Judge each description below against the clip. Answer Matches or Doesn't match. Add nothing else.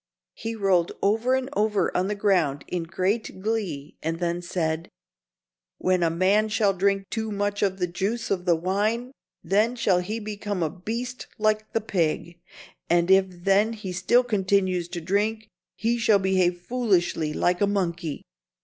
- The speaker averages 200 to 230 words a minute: Doesn't match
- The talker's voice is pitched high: Matches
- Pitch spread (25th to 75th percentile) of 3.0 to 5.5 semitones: Matches